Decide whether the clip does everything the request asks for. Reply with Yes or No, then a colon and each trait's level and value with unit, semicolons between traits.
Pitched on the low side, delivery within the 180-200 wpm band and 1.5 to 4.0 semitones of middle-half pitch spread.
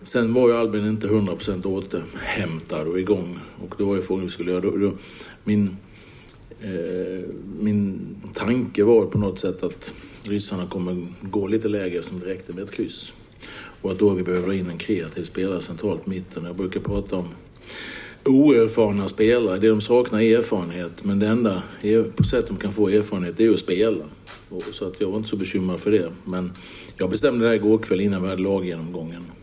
Yes: low, 100 Hz; average, 190 wpm; average, 2.8 semitones